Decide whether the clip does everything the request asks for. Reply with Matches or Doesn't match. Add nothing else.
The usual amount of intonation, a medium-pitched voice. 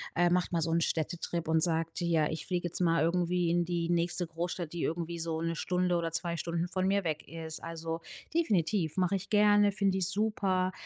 Doesn't match